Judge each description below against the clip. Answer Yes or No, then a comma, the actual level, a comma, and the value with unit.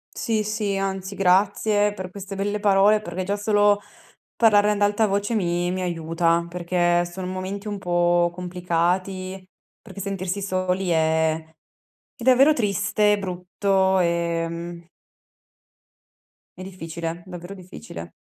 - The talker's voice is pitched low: No, medium, 185 Hz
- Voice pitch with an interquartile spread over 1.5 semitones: Yes, average, 2.7 semitones